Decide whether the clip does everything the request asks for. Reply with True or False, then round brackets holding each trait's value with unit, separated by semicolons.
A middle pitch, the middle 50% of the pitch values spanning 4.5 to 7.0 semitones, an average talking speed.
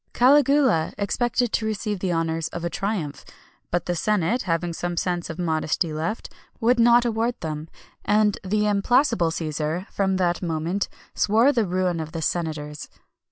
True (180 Hz; 5.0 semitones; 160 wpm)